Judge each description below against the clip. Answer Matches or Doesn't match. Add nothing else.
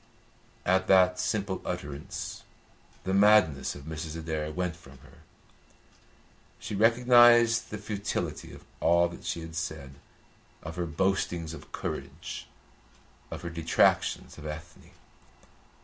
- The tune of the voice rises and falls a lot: Doesn't match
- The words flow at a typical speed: Doesn't match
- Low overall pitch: Matches